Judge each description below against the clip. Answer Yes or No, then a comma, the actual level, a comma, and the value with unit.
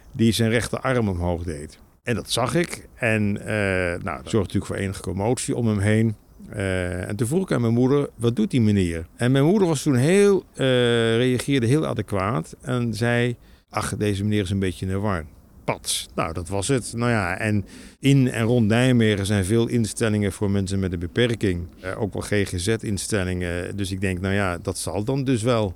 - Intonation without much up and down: No, average, 3.9 semitones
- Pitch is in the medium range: No, low, 105 Hz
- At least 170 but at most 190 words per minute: No, fast, 200 wpm